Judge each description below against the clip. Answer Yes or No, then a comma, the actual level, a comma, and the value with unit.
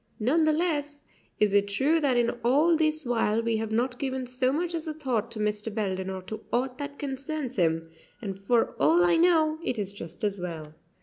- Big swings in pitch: Yes, wide, 6.4 semitones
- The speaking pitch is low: No, very high, 250 Hz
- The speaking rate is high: Yes, fast, 210 wpm